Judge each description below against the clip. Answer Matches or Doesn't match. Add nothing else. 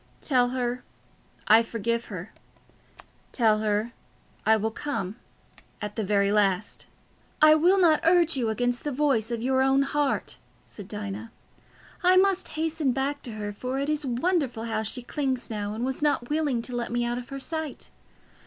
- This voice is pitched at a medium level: Doesn't match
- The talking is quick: Doesn't match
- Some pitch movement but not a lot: Matches